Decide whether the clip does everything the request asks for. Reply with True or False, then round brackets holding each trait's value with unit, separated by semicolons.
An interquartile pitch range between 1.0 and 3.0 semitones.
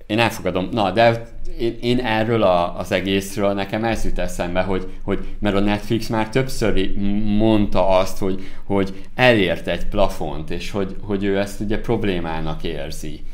True (2.7 semitones)